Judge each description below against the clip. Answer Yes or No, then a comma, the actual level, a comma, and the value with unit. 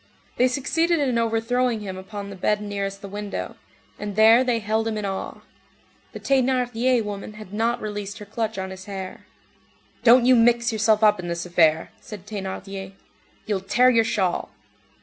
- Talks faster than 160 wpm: Yes, average, 170 wpm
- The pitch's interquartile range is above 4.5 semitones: No, average, 3.1 semitones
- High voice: Yes, high, 215 Hz